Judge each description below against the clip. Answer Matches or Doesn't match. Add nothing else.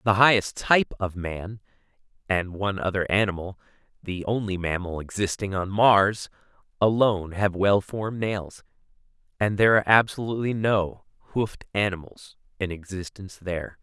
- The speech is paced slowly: Matches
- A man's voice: Matches